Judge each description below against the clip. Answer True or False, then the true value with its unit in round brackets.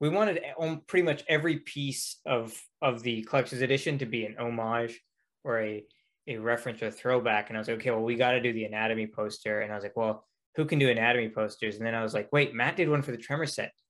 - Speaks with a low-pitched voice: True (120 Hz)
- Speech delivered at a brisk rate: True (255 wpm)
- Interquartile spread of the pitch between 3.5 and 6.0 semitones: True (4.2 semitones)